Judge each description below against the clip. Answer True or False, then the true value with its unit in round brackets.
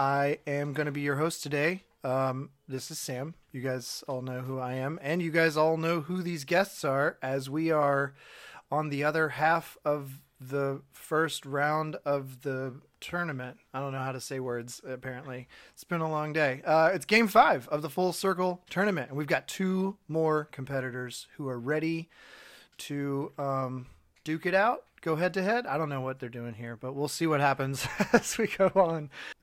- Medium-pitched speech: True (145 Hz)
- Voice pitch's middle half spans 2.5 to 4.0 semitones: True (3.6 semitones)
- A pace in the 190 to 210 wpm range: True (200 wpm)